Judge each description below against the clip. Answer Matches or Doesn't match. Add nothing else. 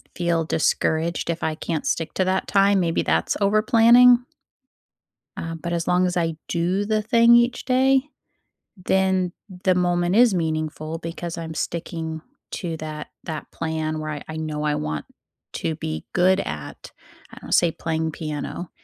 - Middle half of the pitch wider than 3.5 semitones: Doesn't match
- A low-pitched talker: Doesn't match